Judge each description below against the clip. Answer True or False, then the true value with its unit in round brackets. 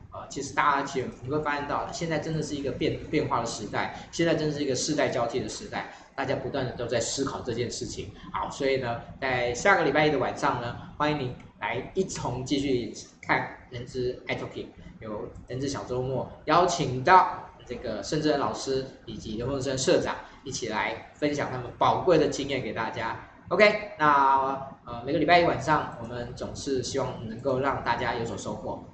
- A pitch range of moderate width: True (3.7 semitones)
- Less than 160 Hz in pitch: True (135 Hz)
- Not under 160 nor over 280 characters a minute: False (305 characters per minute)